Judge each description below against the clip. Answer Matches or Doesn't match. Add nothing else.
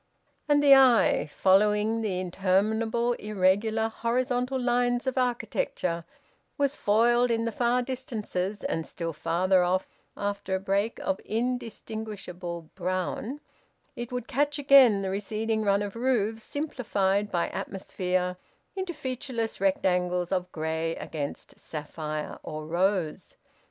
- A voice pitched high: Matches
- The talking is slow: Matches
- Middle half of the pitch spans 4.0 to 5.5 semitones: Matches